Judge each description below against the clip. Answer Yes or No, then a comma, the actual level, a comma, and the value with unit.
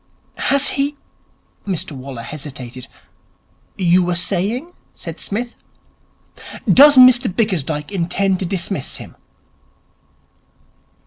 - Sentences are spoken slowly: Yes, slow, 100 wpm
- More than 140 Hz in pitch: Yes, medium, 185 Hz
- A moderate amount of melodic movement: No, wide, 7.9 semitones